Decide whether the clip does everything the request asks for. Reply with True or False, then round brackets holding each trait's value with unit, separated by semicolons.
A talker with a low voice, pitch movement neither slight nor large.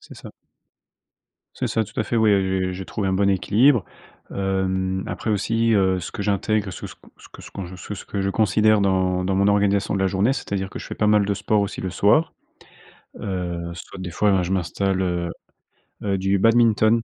False (100 Hz; 2.0 semitones)